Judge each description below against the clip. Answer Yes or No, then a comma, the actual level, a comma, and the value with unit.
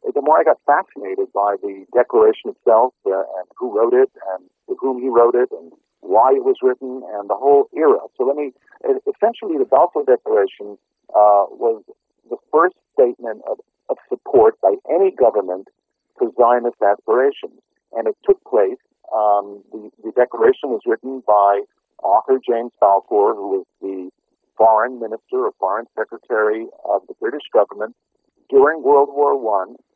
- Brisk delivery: No, average, 160 wpm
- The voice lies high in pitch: Yes, very high, 390 Hz